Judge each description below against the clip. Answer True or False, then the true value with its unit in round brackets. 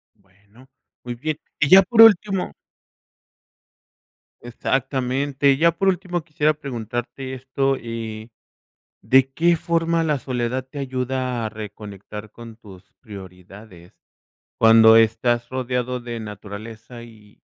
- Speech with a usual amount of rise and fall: True (4.0 semitones)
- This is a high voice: False (125 Hz)